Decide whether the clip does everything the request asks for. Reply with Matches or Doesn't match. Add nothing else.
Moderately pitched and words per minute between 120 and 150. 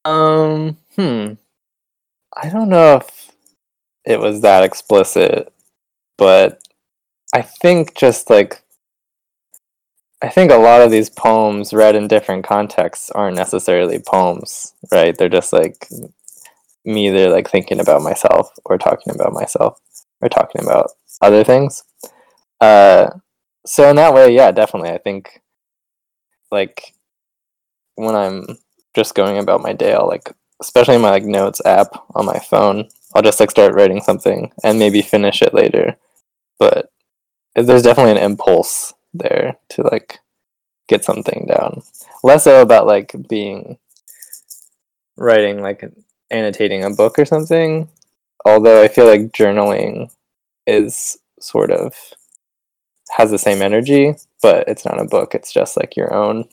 Matches